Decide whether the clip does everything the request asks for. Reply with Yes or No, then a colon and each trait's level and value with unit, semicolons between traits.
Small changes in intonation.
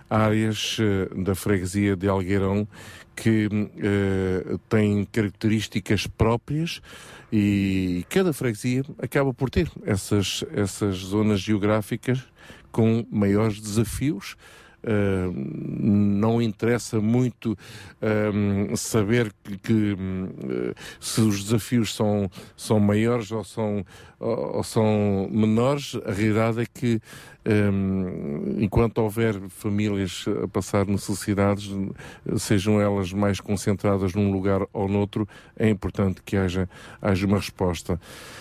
Yes: narrow, 2.2 semitones